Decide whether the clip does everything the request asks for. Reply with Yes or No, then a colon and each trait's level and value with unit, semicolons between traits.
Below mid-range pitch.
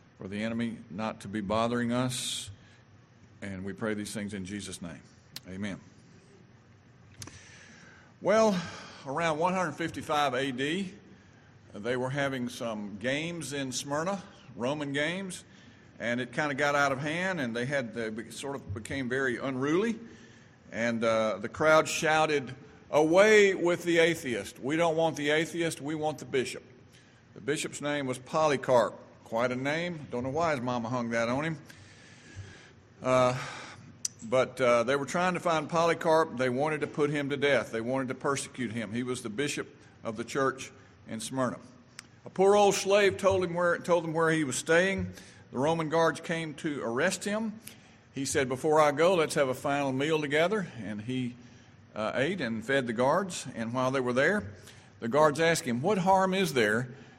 Yes: low, 130 Hz